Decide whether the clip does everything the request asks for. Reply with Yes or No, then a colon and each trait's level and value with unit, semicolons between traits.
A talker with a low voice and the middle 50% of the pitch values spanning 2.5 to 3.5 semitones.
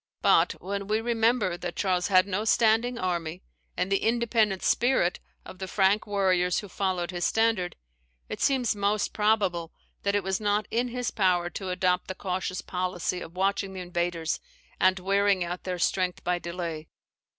No: high, 190 Hz; average, 2.8 semitones